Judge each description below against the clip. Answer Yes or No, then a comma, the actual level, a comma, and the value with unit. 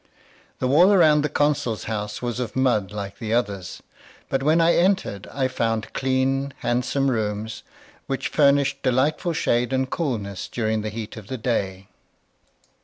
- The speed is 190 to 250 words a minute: No, average, 155 wpm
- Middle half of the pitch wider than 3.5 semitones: Yes, average, 4.4 semitones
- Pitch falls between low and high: No, low, 125 Hz